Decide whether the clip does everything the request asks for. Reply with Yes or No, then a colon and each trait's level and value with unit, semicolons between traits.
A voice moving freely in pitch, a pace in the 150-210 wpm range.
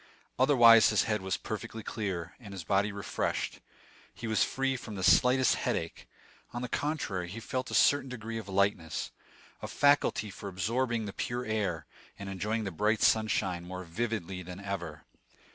No: average, 3.8 semitones; average, 165 wpm